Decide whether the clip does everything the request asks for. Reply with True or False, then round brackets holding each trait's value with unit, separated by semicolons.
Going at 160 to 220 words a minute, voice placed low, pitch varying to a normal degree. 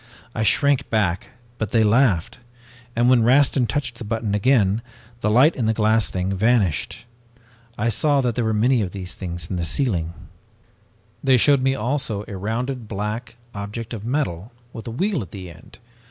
True (180 wpm; 110 Hz; 3.8 semitones)